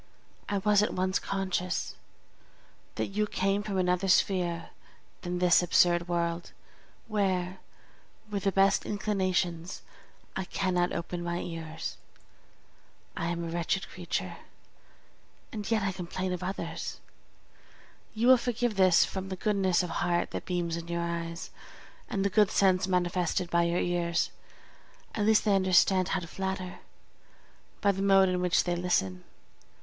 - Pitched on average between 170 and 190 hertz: Yes, medium, 185 Hz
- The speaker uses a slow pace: No, average, 145 wpm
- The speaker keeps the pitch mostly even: Yes, narrow, 2.1 semitones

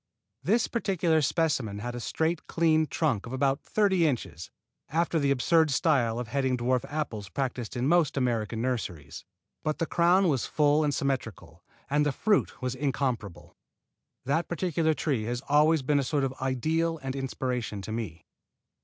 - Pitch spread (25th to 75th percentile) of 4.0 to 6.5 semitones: Yes, average, 4.6 semitones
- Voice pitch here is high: No, medium, 140 Hz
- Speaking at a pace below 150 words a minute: No, average, 160 wpm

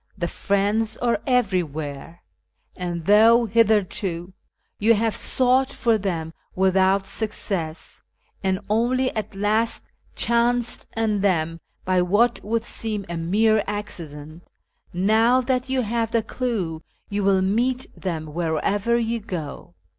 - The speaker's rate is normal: No, slow, 125 wpm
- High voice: Yes, high, 205 Hz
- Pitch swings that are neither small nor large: Yes, average, 4.4 semitones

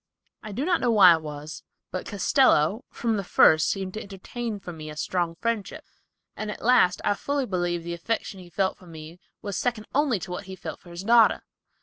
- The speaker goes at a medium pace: No, fast, 210 wpm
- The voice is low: No, high, 190 Hz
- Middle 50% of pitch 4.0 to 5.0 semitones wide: Yes, average, 4.5 semitones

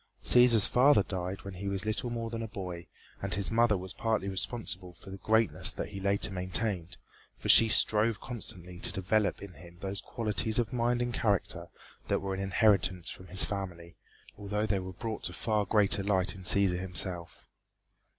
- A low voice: Yes, low, 100 Hz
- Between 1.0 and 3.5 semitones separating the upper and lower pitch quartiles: Yes, average, 3.0 semitones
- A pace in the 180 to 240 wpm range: Yes, average, 185 wpm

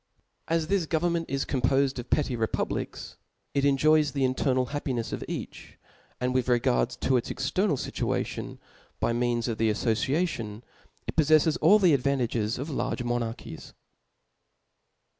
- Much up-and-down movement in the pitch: No, average, 4.3 semitones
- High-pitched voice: No, low, 135 Hz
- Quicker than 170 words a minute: No, average, 140 wpm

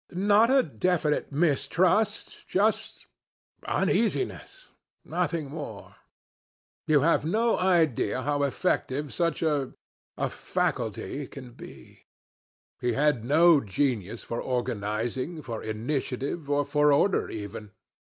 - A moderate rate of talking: No, slow, 105 wpm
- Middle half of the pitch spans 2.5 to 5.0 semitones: No, wide, 5.6 semitones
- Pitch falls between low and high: Yes, medium, 145 Hz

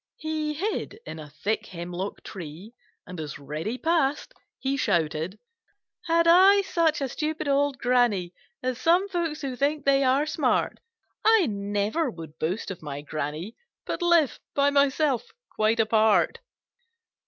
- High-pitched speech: Yes, very high, 255 Hz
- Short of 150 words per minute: Yes, average, 140 wpm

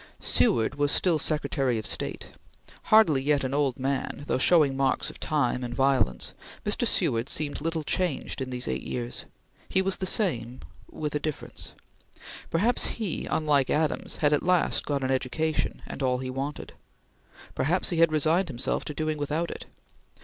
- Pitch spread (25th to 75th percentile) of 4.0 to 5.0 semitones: No, average, 3.4 semitones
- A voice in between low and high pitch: Yes, medium, 145 Hz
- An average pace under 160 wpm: No, average, 170 wpm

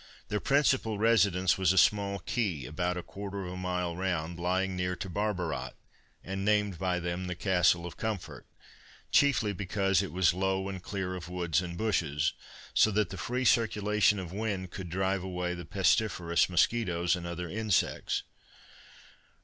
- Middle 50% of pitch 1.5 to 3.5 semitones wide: Yes, narrow, 2.6 semitones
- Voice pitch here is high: No, very low, 95 Hz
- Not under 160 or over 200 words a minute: Yes, average, 165 wpm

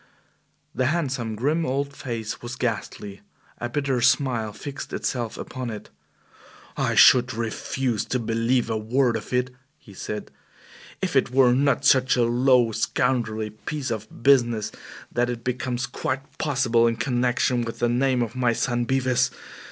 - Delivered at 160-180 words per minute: No, average, 150 wpm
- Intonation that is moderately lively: No, narrow, 2.2 semitones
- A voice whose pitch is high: No, low, 120 Hz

